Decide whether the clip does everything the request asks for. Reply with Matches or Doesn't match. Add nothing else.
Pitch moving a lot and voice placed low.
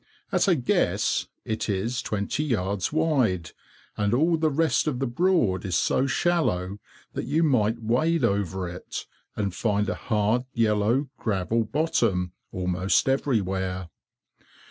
Matches